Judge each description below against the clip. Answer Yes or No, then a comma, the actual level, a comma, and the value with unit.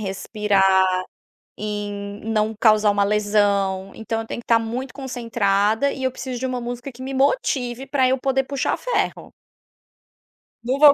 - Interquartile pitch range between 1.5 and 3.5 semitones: No, average, 4.2 semitones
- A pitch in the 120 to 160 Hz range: No, high, 230 Hz